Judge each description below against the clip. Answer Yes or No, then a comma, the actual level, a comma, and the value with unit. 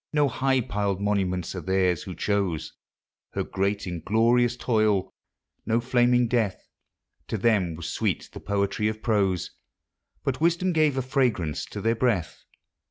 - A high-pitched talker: No, low, 105 Hz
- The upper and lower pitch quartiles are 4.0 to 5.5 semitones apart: Yes, average, 4.5 semitones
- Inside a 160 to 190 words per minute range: No, average, 140 wpm